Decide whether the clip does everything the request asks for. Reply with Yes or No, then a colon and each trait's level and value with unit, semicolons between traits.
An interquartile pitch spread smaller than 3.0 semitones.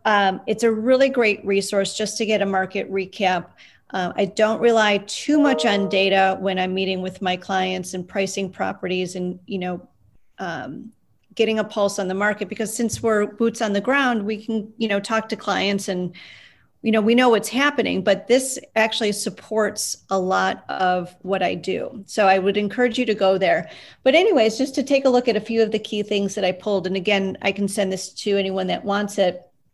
Yes: narrow, 2.6 semitones